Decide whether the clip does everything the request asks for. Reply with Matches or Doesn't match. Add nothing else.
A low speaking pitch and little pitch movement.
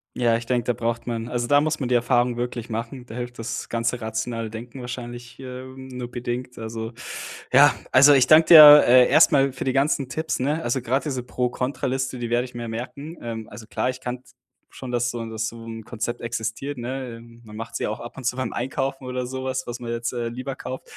Matches